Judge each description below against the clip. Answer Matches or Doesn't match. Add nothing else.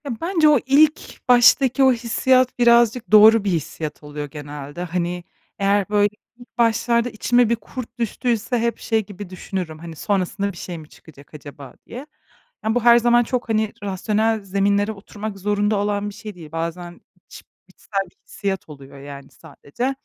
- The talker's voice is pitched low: Doesn't match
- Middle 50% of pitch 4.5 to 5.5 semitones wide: Matches